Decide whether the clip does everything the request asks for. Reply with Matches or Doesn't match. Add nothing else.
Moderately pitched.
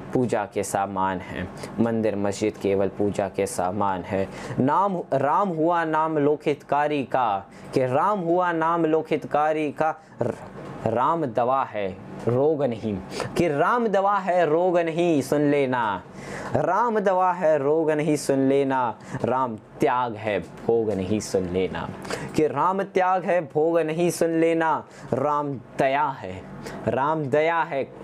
Matches